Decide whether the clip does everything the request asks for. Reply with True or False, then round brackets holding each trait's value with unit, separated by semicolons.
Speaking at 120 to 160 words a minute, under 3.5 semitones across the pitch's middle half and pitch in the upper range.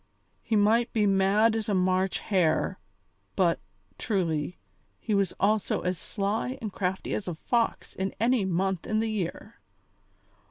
True (150 wpm; 2.8 semitones; 200 Hz)